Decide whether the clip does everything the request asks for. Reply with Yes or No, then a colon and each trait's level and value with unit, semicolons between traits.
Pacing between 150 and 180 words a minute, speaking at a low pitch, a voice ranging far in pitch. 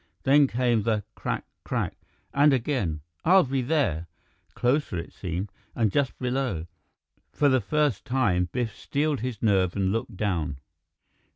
Yes: average, 155 wpm; low, 120 Hz; wide, 6.1 semitones